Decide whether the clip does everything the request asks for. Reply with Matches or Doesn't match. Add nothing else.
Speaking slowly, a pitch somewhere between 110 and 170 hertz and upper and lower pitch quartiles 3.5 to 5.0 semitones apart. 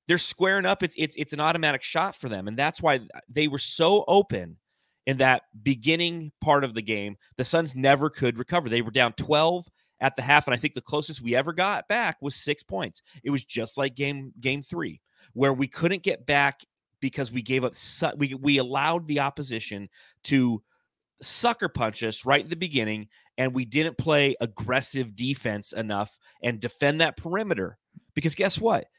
Doesn't match